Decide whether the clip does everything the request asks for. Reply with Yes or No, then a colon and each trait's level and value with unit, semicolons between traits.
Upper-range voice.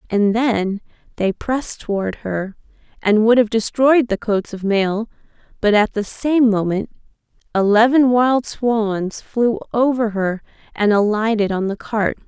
Yes: high, 220 Hz